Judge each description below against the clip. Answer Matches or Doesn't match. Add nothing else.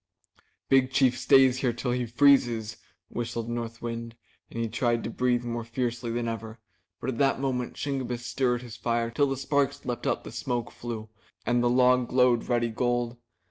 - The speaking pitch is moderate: Doesn't match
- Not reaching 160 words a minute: Doesn't match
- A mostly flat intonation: Matches